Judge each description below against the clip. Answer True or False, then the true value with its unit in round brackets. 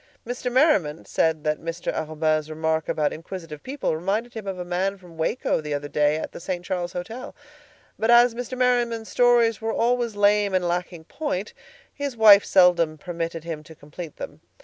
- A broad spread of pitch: True (6.2 semitones)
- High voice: False (180 Hz)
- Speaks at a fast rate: False (175 wpm)